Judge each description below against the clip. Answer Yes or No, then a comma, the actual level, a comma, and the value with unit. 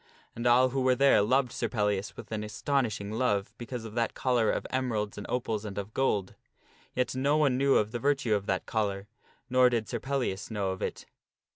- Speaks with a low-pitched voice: Yes, low, 115 Hz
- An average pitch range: Yes, average, 3.7 semitones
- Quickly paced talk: Yes, fast, 215 wpm